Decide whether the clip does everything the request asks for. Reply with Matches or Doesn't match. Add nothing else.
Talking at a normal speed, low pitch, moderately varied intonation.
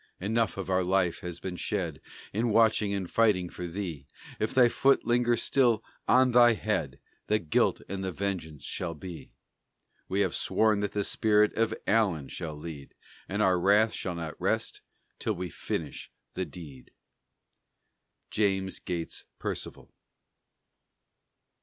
Matches